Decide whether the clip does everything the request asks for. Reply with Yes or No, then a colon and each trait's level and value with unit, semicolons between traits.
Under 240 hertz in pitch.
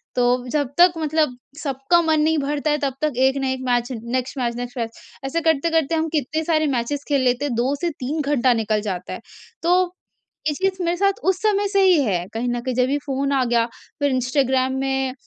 No: very high, 275 Hz